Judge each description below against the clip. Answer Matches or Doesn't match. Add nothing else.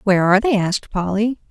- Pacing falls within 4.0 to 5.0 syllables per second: Doesn't match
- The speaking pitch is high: Matches